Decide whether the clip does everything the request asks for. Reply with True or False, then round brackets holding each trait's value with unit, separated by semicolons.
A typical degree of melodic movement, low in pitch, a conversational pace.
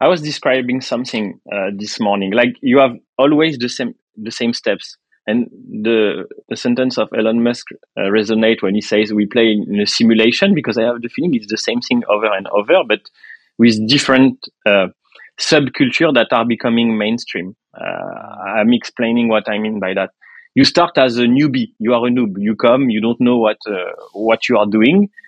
True (3.3 semitones; 120 Hz; 195 wpm)